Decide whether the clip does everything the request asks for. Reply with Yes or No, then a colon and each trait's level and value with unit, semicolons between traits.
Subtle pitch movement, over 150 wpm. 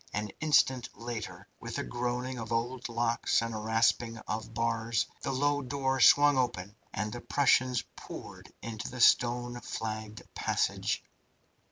No: narrow, 2.2 semitones; average, 145 wpm